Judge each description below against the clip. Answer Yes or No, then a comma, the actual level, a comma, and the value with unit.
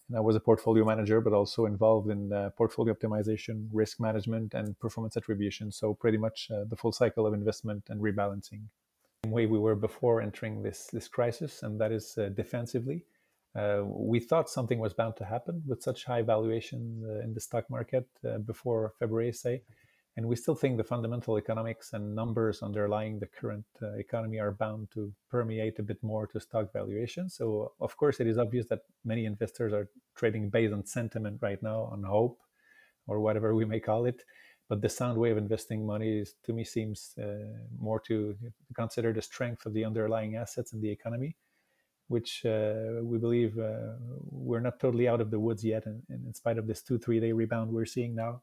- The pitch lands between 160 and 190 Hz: No, low, 110 Hz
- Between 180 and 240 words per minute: Yes, average, 200 wpm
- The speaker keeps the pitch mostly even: Yes, narrow, 1.5 semitones